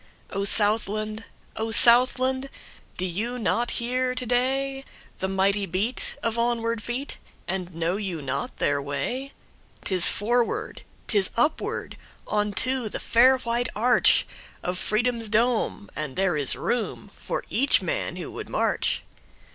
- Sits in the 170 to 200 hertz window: No, high, 225 Hz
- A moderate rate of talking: No, slow, 115 wpm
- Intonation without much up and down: No, average, 4.3 semitones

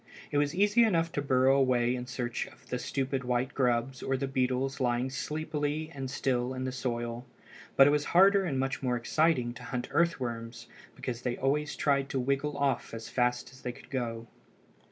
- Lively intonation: No, average, 2.7 semitones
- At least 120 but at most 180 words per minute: No, average, 195 wpm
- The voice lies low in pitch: Yes, low, 130 Hz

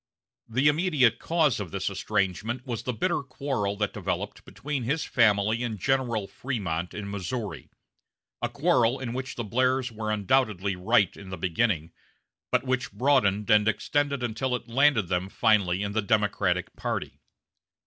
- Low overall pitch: Yes, low, 115 Hz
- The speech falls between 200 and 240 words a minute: No, average, 155 wpm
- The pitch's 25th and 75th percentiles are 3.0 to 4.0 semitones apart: No, average, 4.4 semitones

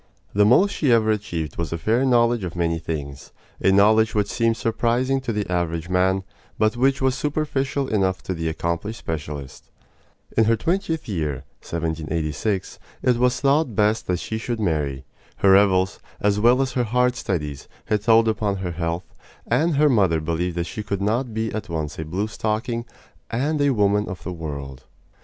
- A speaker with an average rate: Yes, average, 180 wpm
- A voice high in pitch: No, low, 105 Hz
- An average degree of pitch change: No, wide, 5.9 semitones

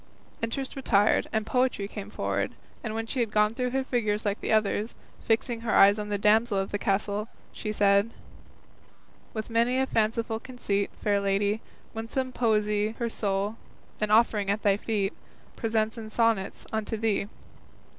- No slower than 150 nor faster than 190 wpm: Yes, average, 165 wpm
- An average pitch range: No, narrow, 2.0 semitones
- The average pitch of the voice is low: No, high, 215 Hz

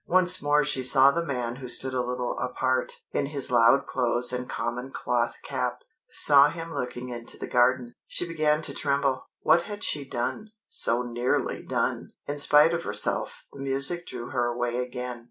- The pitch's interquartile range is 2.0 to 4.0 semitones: Yes, average, 3.1 semitones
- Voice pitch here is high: No, low, 130 Hz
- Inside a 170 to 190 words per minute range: Yes, average, 180 wpm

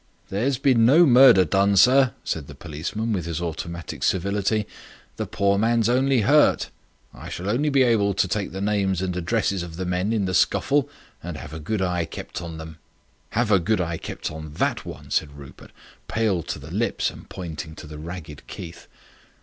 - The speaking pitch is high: No, very low, 95 Hz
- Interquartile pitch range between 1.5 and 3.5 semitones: No, average, 5.2 semitones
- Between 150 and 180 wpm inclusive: No, average, 195 wpm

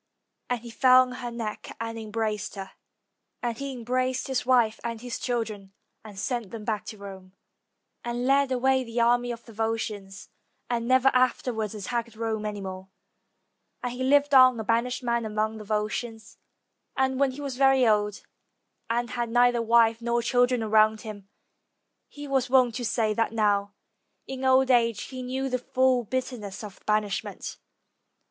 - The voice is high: Yes, high, 235 Hz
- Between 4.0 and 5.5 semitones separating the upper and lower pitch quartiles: No, average, 2.9 semitones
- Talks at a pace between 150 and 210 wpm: Yes, average, 170 wpm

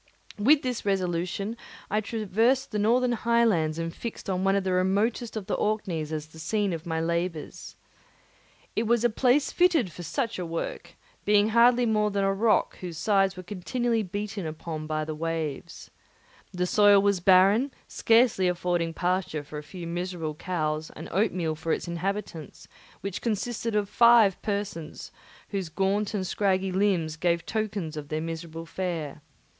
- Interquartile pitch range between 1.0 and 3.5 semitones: No, average, 4.3 semitones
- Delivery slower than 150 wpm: No, average, 165 wpm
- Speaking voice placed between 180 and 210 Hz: Yes, high, 190 Hz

